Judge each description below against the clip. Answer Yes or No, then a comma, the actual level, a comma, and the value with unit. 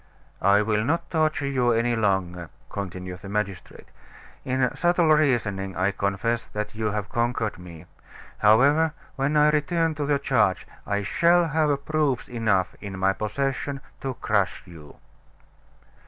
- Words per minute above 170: No, average, 140 wpm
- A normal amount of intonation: No, wide, 6.5 semitones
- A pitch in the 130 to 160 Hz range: No, low, 115 Hz